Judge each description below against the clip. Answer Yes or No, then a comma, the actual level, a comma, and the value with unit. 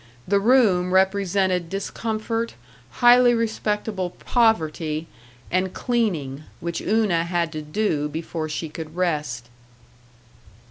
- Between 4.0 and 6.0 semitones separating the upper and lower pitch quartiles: Yes, average, 5.2 semitones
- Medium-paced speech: No, slow, 100 wpm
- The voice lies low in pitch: No, medium, 185 Hz